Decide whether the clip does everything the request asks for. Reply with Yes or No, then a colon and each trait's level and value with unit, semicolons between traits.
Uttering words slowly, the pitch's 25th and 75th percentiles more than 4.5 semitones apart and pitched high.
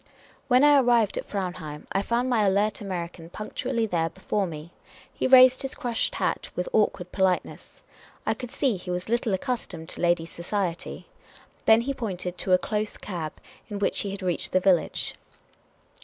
No: average, 170 wpm; average, 4.9 semitones; high, 200 Hz